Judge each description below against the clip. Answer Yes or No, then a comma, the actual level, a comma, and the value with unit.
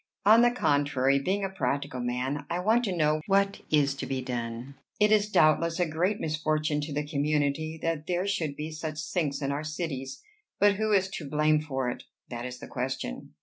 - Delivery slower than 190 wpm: No, average, 200 wpm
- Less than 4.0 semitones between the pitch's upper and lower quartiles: No, average, 4.4 semitones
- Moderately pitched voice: Yes, medium, 155 Hz